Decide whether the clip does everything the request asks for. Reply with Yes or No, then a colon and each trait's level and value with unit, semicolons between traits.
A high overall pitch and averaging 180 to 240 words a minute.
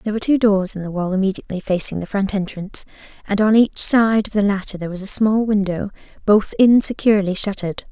Yes: high, 200 Hz; fast, 205 wpm